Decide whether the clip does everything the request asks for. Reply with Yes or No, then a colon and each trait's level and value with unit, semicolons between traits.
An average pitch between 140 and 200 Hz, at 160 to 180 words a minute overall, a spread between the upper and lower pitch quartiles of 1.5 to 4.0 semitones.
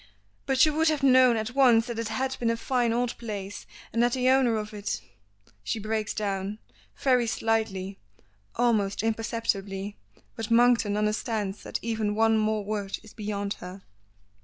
No: high, 220 Hz; average, 165 wpm; average, 2.7 semitones